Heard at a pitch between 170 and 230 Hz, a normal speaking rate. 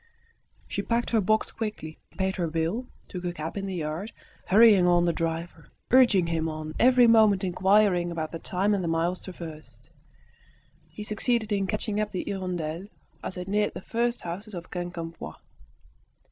Yes: medium, 185 Hz; average, 170 wpm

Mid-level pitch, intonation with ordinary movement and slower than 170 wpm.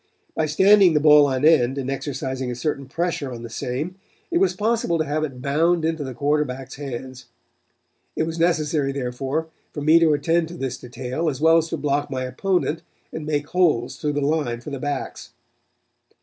No: medium, 145 Hz; average, 3.5 semitones; average, 190 wpm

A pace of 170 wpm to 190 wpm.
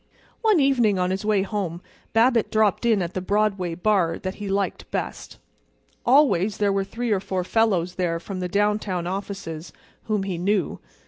Yes: average, 175 wpm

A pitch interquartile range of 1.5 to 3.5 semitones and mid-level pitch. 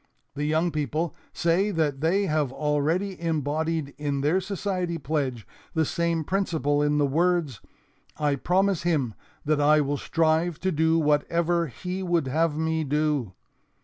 Yes: narrow, 2.6 semitones; medium, 160 Hz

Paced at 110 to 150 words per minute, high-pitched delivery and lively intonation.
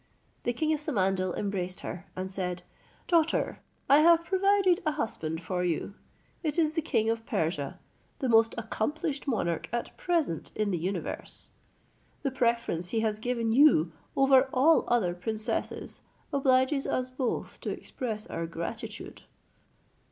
Yes: average, 145 wpm; high, 230 Hz; wide, 7.4 semitones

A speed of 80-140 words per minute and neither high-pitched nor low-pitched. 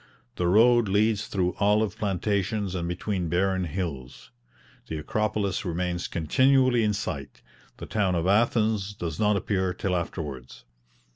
No: slow, 135 wpm; very low, 95 Hz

